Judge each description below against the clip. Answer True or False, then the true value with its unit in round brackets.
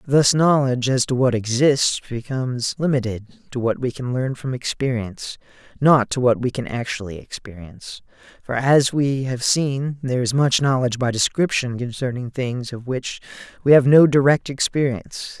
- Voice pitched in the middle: False (130 Hz)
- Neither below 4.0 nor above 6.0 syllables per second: True (5.0 syllables/s)